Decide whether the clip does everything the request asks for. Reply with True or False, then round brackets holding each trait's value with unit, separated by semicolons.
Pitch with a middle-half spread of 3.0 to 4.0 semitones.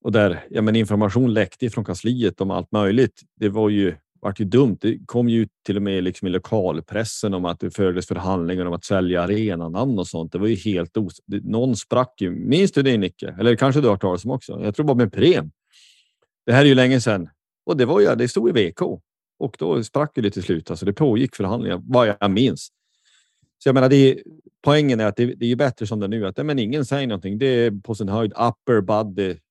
False (4.4 semitones)